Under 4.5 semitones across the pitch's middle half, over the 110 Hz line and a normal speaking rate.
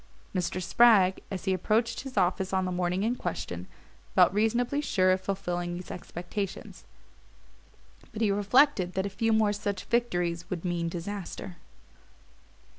Yes: average, 3.3 semitones; high, 190 Hz; average, 145 wpm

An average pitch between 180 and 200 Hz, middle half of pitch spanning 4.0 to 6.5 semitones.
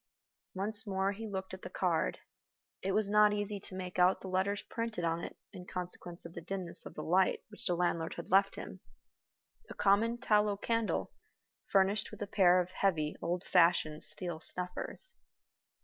No: high, 190 Hz; narrow, 2.5 semitones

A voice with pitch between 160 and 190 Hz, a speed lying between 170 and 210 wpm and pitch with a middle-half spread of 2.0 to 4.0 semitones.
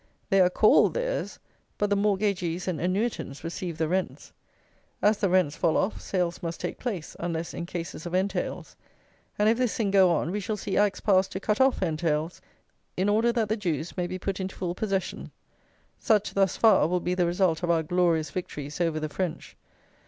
Yes: medium, 185 Hz; average, 195 wpm; average, 3.1 semitones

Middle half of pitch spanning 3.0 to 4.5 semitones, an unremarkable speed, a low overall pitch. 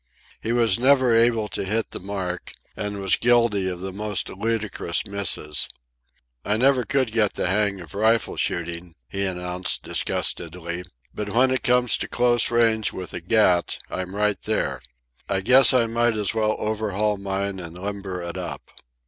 Yes: average, 3.7 semitones; average, 165 wpm; low, 105 Hz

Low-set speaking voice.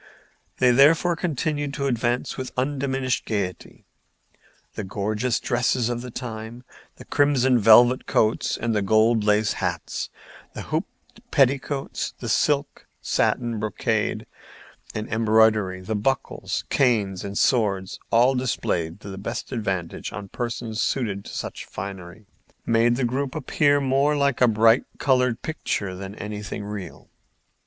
Yes: low, 115 Hz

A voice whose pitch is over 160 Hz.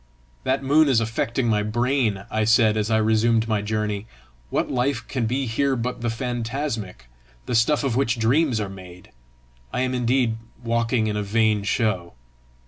No: low, 115 Hz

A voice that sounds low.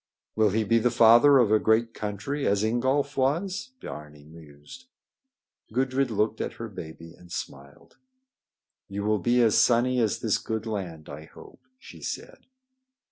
Yes: low, 110 Hz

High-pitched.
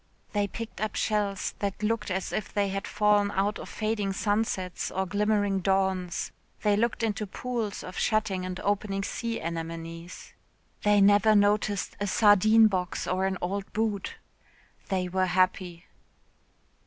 Yes: high, 200 Hz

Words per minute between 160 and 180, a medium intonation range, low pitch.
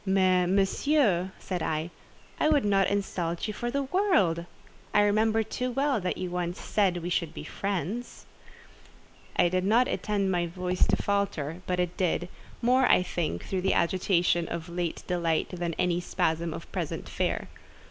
No: average, 170 wpm; average, 3.1 semitones; medium, 185 Hz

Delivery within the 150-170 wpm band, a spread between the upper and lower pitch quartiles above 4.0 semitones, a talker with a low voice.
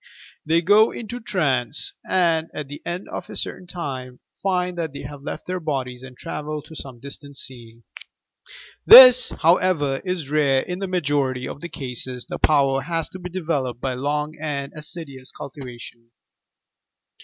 No: average, 160 wpm; average, 4.8 semitones; medium, 145 Hz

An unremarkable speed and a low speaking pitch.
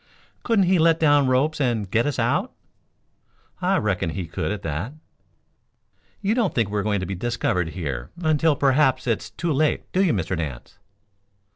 Yes: average, 180 wpm; low, 120 Hz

